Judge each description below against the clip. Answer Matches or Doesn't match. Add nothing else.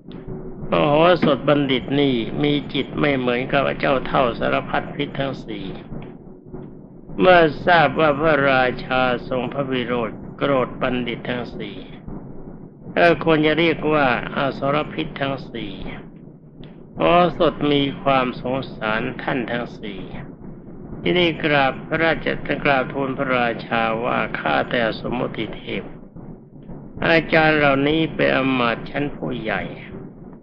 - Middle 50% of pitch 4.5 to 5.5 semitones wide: Doesn't match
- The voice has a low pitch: Doesn't match